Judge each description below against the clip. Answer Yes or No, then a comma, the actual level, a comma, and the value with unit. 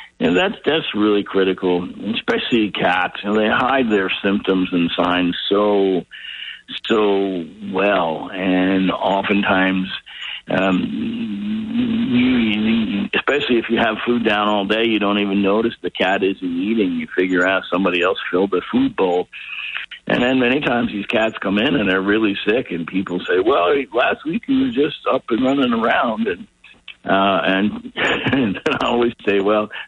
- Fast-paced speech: No, average, 160 wpm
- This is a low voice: Yes, low, 105 Hz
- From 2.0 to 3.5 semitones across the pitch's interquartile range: No, average, 4.1 semitones